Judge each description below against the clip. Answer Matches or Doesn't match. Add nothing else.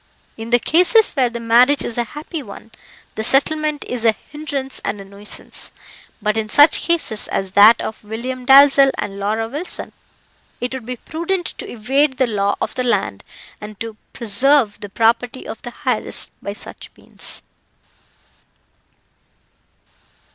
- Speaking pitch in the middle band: Doesn't match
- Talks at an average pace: Matches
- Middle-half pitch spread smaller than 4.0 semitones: Doesn't match